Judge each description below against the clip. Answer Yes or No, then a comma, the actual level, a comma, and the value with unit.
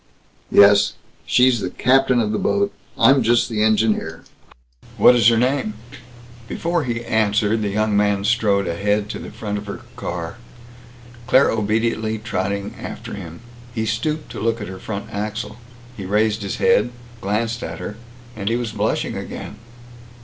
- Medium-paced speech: Yes, average, 160 wpm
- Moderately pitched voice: No, low, 110 Hz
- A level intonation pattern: Yes, narrow, 2.3 semitones